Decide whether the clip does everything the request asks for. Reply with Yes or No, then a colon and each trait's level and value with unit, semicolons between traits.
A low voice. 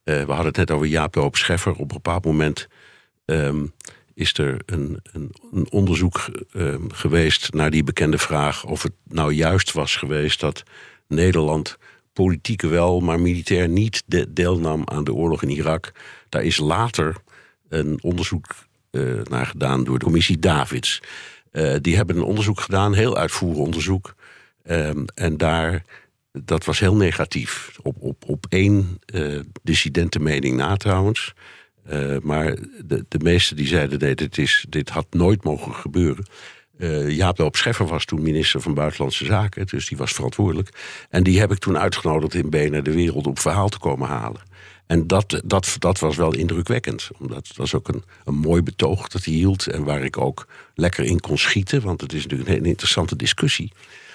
Yes: very low, 85 Hz